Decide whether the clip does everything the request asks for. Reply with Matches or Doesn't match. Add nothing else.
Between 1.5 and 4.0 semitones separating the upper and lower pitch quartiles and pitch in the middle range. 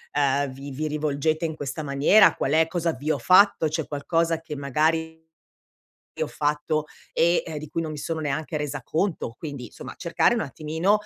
Matches